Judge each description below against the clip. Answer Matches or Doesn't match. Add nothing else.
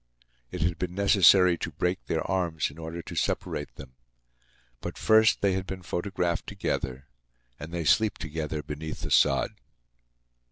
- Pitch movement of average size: Matches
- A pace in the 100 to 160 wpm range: Matches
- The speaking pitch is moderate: Doesn't match